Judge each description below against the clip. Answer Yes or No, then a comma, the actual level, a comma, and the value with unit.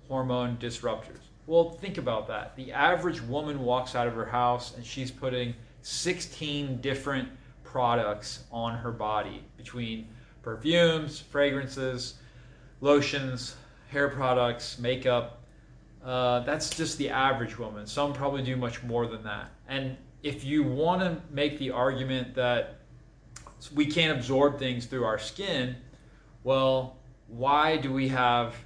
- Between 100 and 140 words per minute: Yes, slow, 135 wpm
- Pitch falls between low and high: No, low, 130 Hz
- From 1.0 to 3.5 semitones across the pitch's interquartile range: Yes, average, 2.8 semitones